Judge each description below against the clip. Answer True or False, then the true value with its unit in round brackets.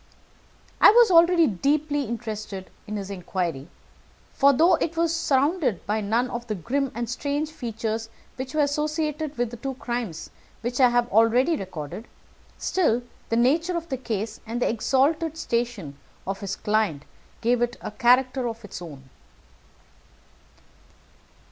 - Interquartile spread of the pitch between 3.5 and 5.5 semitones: True (5.2 semitones)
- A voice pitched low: False (240 Hz)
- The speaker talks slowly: False (150 wpm)